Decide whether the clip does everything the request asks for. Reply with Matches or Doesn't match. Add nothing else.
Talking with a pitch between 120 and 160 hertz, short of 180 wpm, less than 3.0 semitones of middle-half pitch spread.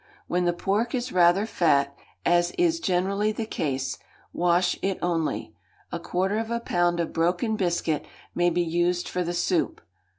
Doesn't match